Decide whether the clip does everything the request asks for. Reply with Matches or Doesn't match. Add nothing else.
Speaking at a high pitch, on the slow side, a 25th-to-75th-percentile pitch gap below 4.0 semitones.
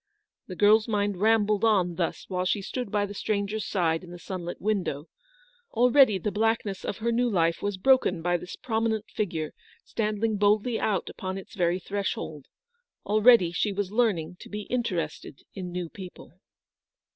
Doesn't match